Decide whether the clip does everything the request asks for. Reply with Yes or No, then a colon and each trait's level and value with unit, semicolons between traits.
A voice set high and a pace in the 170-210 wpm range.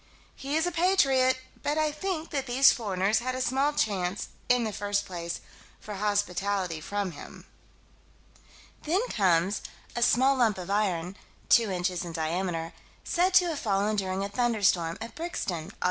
No: high, 210 Hz; average, 160 wpm